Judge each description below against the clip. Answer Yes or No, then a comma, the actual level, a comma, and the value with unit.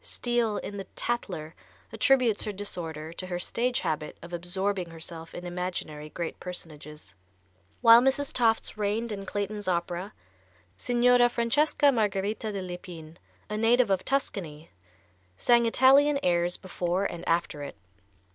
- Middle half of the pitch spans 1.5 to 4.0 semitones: No, wide, 5.4 semitones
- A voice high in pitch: Yes, high, 195 Hz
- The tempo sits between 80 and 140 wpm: Yes, slow, 135 wpm